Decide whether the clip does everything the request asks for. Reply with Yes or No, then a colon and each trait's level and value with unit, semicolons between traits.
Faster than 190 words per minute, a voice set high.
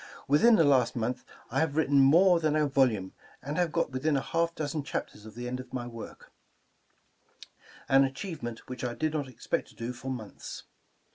No: average, 200 wpm; low, 135 Hz